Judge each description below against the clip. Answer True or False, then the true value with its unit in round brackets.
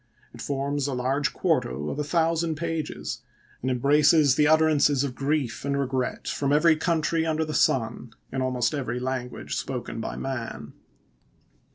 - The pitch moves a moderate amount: True (3.3 semitones)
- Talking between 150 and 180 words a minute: True (155 wpm)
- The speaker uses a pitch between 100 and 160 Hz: True (140 Hz)